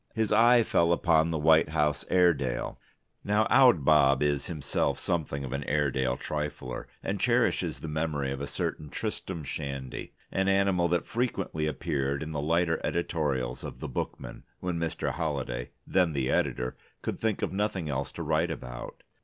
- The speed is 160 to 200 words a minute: Yes, average, 165 wpm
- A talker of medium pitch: No, very low, 75 Hz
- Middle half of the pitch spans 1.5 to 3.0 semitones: No, average, 4.1 semitones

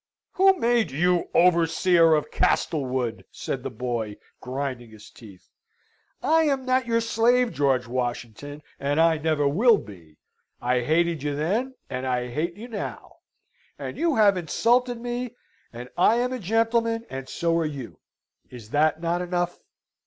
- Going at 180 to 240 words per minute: No, average, 155 wpm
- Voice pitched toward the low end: No, medium, 165 Hz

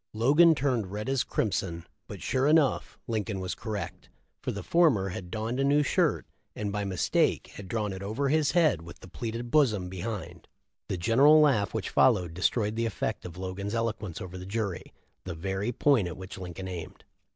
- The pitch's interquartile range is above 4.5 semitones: Yes, average, 5.2 semitones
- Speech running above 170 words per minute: Yes, average, 190 wpm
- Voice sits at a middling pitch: No, low, 105 Hz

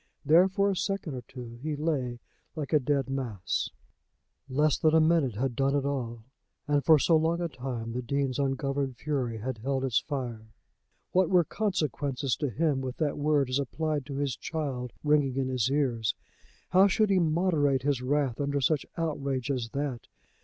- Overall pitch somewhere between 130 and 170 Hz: Yes, medium, 140 Hz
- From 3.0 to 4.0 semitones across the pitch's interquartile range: Yes, average, 3.3 semitones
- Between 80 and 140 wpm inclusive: No, average, 180 wpm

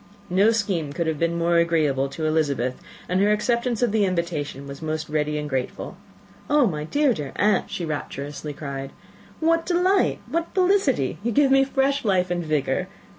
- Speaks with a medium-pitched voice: Yes, medium, 170 Hz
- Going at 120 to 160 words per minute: No, average, 175 wpm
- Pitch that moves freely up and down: Yes, wide, 8.0 semitones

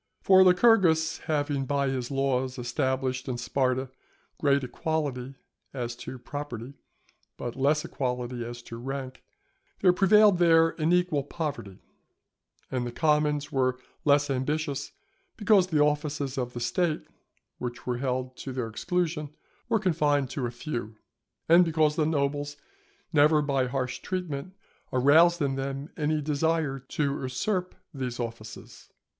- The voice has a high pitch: No, medium, 140 Hz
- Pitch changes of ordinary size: Yes, average, 3.7 semitones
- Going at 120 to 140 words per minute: Yes, slow, 135 wpm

